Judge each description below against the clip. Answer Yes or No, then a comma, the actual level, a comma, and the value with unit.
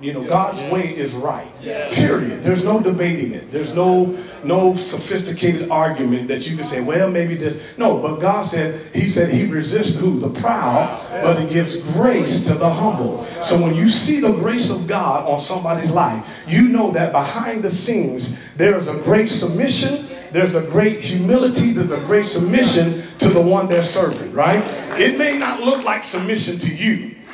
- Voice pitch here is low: No, medium, 180 Hz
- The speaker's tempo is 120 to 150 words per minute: No, average, 185 wpm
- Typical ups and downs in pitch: Yes, average, 4.1 semitones